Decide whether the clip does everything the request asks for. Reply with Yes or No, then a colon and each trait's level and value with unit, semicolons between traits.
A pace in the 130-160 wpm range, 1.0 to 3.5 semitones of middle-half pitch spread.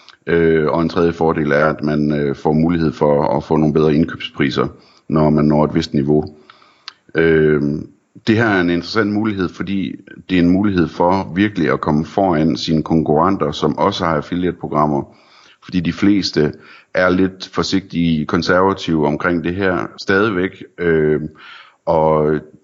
Yes: slow, 145 wpm; average, 3.1 semitones